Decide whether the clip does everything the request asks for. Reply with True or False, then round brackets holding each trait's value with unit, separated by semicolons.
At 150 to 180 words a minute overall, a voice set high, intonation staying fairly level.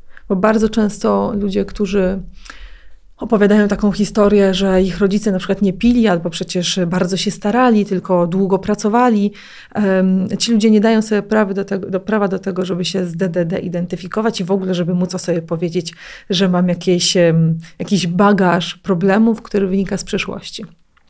True (160 wpm; 195 Hz; 2.2 semitones)